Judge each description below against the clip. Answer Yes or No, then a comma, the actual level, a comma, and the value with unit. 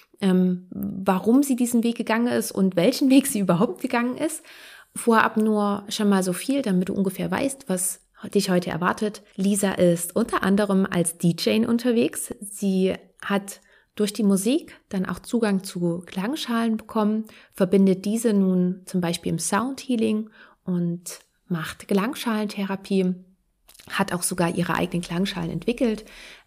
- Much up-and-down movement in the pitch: No, average, 3.6 semitones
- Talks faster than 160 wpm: No, average, 140 wpm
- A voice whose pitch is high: Yes, high, 200 Hz